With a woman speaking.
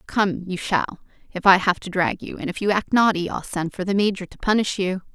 Yes: female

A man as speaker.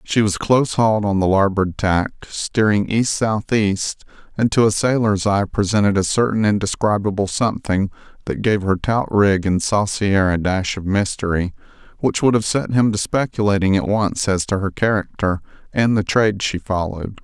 Yes: male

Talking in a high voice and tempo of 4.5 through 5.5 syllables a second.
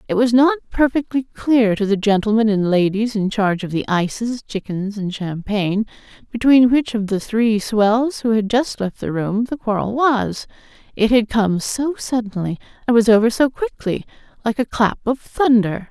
Yes: high, 225 Hz; 4.7 syllables/s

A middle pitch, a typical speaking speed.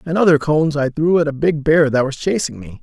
No: medium, 150 Hz; fast, 275 wpm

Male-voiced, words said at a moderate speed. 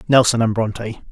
Yes: male; average, 160 wpm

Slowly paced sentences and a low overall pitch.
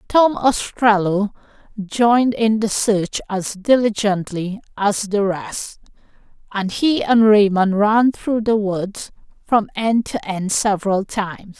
No: slow, 130 wpm; high, 210 Hz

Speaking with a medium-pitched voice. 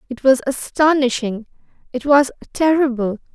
No: very high, 260 Hz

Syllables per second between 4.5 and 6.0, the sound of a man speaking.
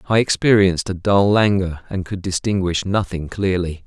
Yes: 5.0 syllables/s; male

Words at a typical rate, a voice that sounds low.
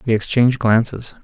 Yes: average, 145 wpm; low, 115 Hz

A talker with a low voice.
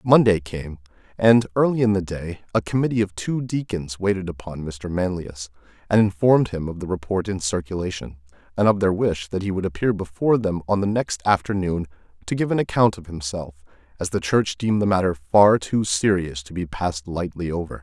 Yes: very low, 95 Hz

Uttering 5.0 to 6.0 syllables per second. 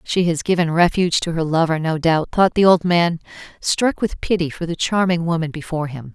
Yes: 5.5 syllables/s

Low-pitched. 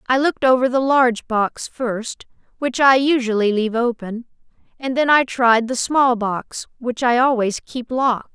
No: high, 245 Hz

